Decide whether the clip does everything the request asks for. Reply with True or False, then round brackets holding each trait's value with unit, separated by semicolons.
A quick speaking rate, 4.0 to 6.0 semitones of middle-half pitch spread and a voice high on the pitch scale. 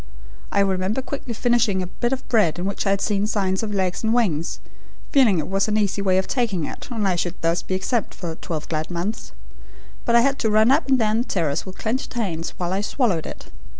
True (235 wpm; 4.3 semitones; 200 Hz)